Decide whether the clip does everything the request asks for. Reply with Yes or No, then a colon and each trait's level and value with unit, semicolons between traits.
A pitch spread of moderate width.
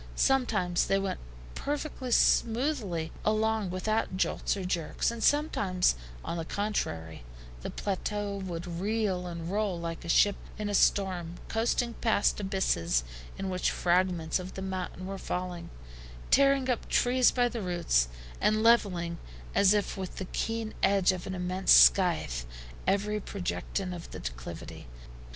Yes: average, 3.5 semitones